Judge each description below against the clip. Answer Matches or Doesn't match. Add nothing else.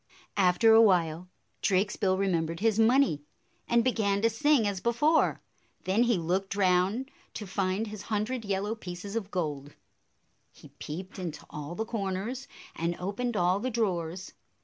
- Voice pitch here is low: Doesn't match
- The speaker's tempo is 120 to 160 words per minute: Matches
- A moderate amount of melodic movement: Matches